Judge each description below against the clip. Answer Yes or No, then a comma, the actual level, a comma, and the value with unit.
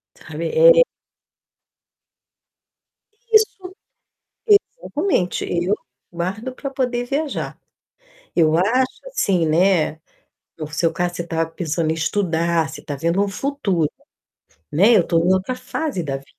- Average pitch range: No, wide, 7.8 semitones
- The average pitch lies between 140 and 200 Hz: Yes, medium, 185 Hz